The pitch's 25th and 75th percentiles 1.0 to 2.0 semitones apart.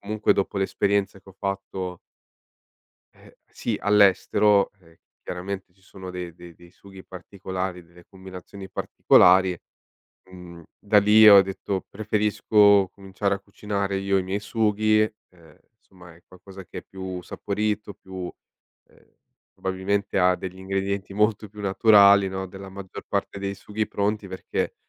Yes: narrow, 1.6 semitones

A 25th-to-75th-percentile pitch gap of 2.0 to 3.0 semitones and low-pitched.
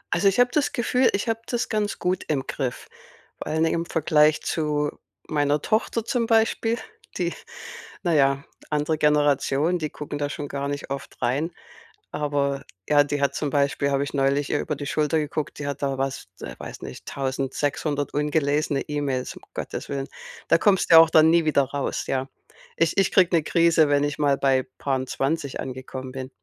No: average, 2.7 semitones; medium, 145 Hz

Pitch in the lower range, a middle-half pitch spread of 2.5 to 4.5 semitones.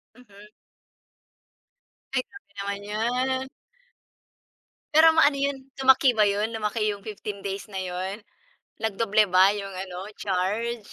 No: high, 210 Hz; average, 4.0 semitones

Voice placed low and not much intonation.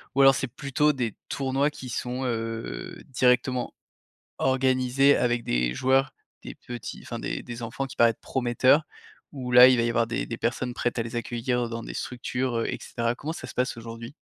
Yes: low, 125 Hz; narrow, 2.0 semitones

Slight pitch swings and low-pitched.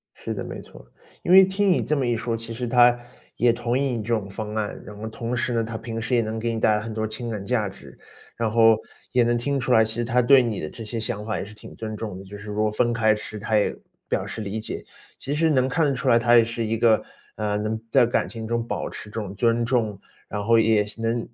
Yes: narrow, 1.9 semitones; low, 115 Hz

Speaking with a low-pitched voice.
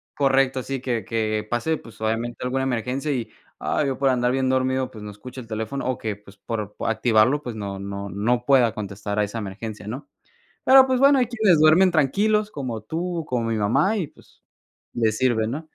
Yes: low, 125 Hz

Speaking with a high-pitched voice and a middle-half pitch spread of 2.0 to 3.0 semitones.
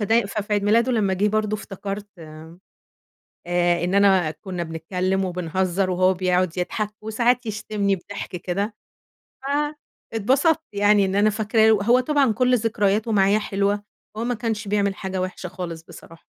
Yes: high, 200 Hz; average, 2.7 semitones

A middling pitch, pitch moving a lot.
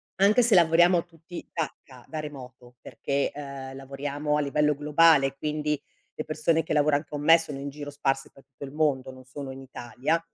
No: medium, 145 Hz; narrow, 2.6 semitones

